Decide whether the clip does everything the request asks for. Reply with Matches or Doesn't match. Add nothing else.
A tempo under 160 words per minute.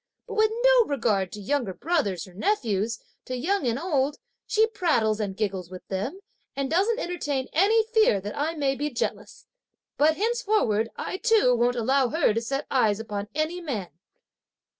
Doesn't match